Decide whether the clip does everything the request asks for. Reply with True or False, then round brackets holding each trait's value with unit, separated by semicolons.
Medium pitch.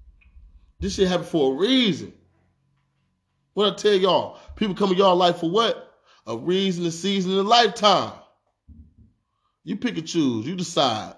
True (170 Hz)